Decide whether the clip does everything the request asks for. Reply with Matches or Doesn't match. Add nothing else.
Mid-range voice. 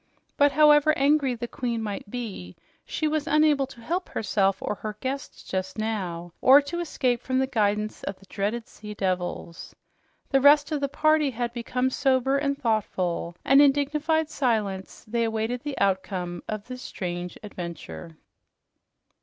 Doesn't match